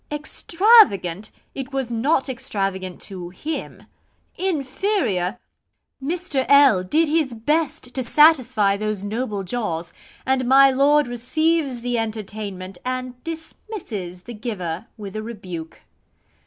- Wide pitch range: Yes, wide, 6.6 semitones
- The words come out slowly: Yes, slow, 115 wpm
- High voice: Yes, high, 245 Hz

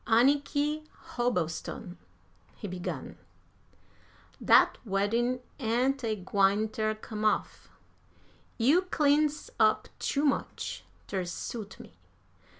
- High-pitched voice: Yes, high, 230 Hz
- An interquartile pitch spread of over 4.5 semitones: Yes, average, 5.3 semitones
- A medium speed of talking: No, slow, 95 wpm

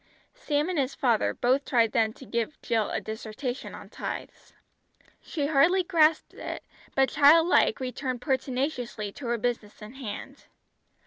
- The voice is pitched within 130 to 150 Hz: No, very high, 260 Hz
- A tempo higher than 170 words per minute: No, average, 150 wpm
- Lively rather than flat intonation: No, average, 4.0 semitones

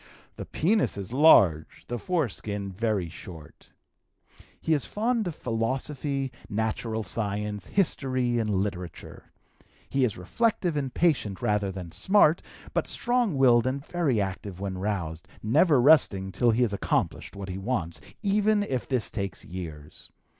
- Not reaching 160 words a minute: Yes, average, 140 wpm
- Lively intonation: Yes, wide, 7.2 semitones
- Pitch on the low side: Yes, low, 115 Hz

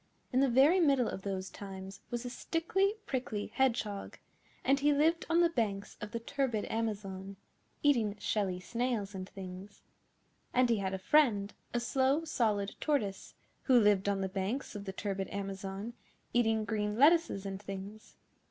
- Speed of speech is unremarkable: Yes, average, 160 wpm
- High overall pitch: Yes, high, 215 Hz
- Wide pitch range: No, average, 5.0 semitones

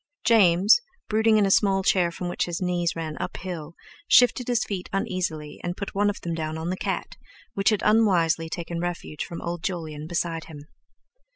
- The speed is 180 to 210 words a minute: Yes, average, 185 wpm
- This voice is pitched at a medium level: Yes, medium, 175 Hz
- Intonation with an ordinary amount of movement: Yes, average, 3.1 semitones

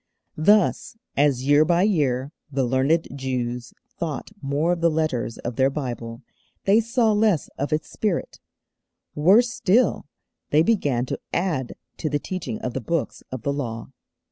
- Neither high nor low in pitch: Yes, medium, 150 Hz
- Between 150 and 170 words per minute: Yes, average, 155 wpm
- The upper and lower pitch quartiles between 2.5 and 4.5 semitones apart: No, wide, 5.6 semitones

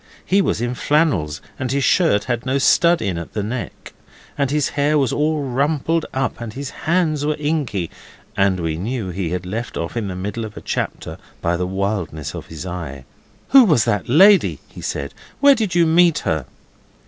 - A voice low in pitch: Yes, low, 120 Hz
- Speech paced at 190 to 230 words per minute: Yes, average, 195 wpm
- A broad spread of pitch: Yes, wide, 8.5 semitones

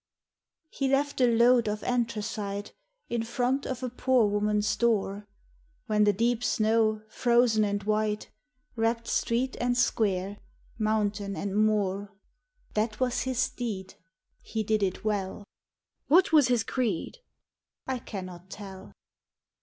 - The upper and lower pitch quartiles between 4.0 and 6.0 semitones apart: No, average, 2.9 semitones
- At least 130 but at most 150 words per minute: Yes, slow, 135 wpm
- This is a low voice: No, high, 220 Hz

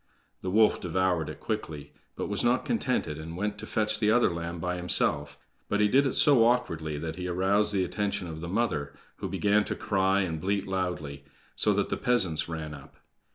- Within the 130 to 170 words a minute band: No, average, 200 wpm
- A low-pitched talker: Yes, very low, 95 Hz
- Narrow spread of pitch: No, average, 4.5 semitones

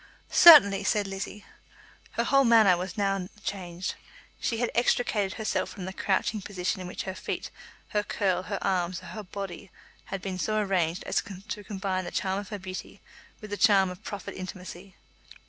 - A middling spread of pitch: No, narrow, 2.0 semitones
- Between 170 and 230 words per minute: Yes, average, 180 wpm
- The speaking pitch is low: No, high, 195 Hz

